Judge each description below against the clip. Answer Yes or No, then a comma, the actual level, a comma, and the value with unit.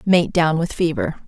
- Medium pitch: Yes, medium, 170 Hz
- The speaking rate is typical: Yes, average, 190 wpm